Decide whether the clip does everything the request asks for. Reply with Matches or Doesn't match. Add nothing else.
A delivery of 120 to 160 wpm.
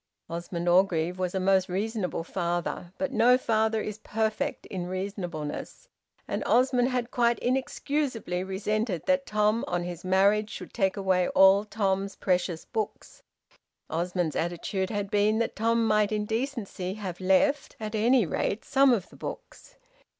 Matches